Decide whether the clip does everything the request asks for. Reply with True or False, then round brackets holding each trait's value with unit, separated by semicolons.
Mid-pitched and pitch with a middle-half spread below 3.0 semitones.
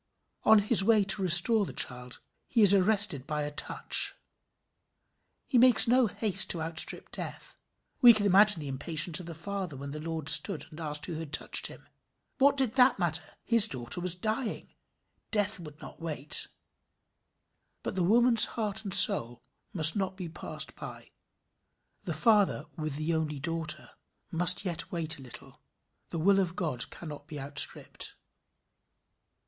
False (175 Hz; 5.2 semitones)